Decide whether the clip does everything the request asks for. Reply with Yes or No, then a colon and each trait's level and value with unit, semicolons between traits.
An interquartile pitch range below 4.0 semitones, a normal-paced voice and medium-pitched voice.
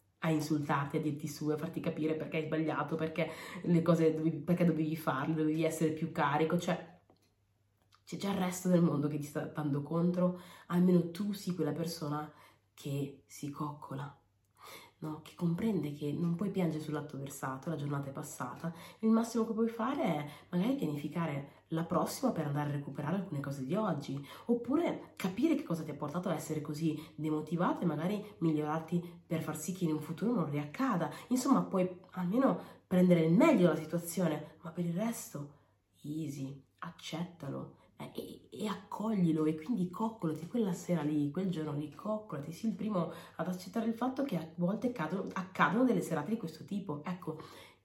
No: average, 3.4 semitones; fast, 180 wpm; medium, 160 Hz